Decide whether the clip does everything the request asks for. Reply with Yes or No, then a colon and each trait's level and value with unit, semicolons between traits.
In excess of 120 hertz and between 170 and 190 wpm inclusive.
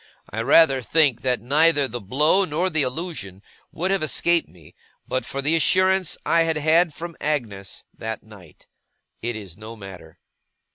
No: medium, 140 Hz; average, 160 wpm